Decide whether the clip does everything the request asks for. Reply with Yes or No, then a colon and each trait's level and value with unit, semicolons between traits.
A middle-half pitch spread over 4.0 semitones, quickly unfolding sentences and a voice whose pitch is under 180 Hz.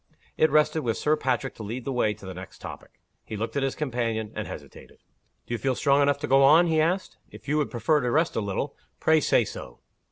Yes: average, 5.1 semitones; fast, 245 wpm; low, 135 Hz